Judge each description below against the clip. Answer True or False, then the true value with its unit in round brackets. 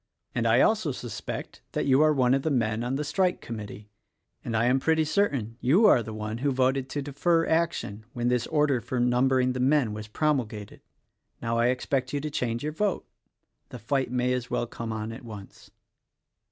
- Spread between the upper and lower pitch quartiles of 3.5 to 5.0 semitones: True (3.9 semitones)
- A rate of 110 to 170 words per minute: False (200 wpm)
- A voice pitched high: False (125 Hz)